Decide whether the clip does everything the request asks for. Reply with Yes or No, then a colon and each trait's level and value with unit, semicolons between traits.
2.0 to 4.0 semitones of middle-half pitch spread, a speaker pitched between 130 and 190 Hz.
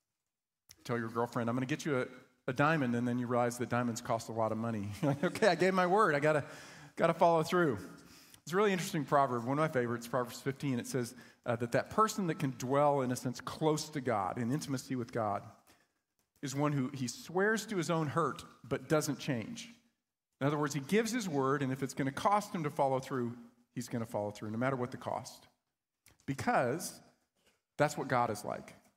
No: average, 4.4 semitones; low, 135 Hz